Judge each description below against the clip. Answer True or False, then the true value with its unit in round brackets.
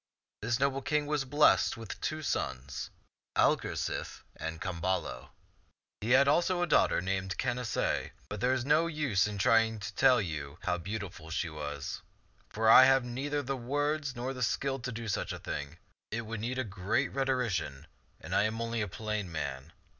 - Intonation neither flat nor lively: False (6.1 semitones)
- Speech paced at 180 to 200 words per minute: True (185 wpm)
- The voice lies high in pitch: False (115 Hz)